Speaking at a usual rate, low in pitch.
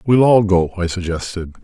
Yes: average, 185 wpm; very low, 95 Hz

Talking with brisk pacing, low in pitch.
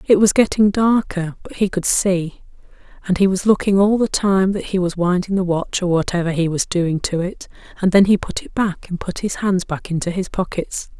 No: fast, 230 wpm; medium, 185 Hz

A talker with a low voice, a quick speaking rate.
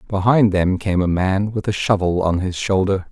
Yes: very low, 95 Hz; fast, 210 wpm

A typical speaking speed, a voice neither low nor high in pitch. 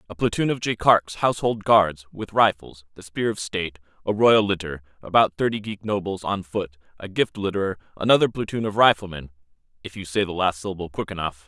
No: average, 190 wpm; very low, 95 Hz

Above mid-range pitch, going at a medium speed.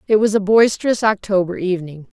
Yes: high, 200 Hz; average, 165 wpm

